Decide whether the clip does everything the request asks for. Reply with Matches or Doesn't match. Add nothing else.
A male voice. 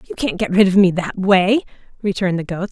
Doesn't match